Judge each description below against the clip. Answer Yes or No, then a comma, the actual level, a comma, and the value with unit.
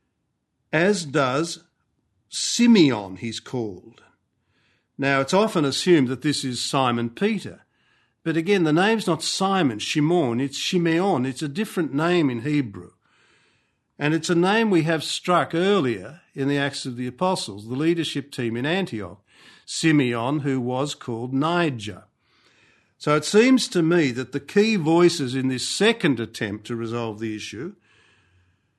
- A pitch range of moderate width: No, wide, 5.8 semitones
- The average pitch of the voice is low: No, medium, 145 Hz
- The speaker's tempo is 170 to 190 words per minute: No, average, 145 wpm